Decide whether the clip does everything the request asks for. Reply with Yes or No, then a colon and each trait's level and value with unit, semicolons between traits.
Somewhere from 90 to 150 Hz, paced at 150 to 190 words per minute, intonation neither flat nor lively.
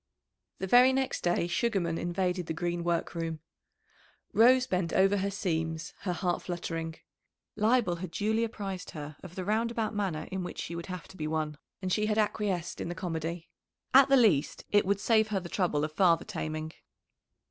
No: medium, 180 Hz; average, 185 wpm; average, 4.0 semitones